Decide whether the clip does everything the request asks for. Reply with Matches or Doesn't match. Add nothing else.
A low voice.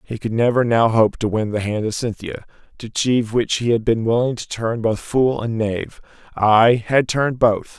Matches